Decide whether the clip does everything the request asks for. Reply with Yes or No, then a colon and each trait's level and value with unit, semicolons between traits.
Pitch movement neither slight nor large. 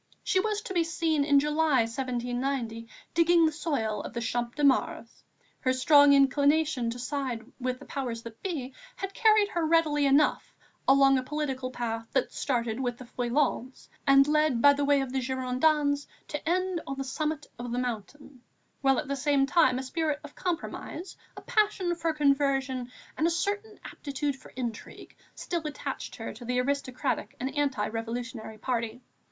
Yes: average, 3.6 semitones